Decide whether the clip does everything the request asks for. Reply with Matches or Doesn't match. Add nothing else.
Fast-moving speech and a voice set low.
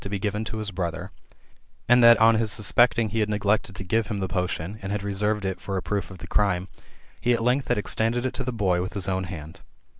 Matches